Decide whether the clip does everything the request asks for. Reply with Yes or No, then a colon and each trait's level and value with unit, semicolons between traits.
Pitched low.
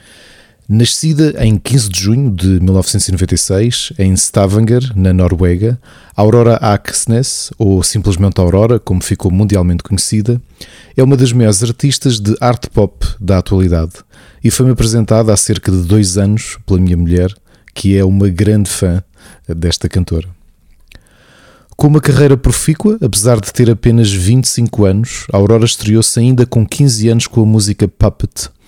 Yes: low, 105 Hz